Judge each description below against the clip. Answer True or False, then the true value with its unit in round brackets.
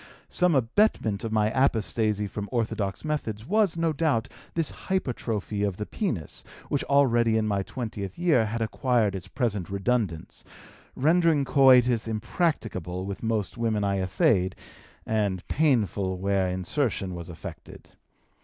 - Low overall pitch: True (110 Hz)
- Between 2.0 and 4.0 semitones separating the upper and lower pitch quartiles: False (5.3 semitones)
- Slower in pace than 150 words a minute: True (135 wpm)